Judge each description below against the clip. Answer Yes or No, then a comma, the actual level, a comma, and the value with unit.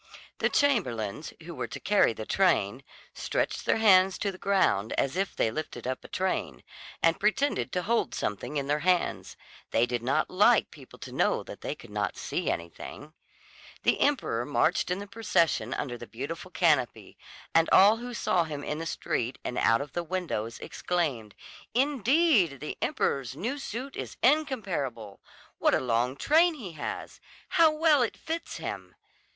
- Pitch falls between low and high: Yes, medium, 170 Hz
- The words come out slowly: No, average, 170 wpm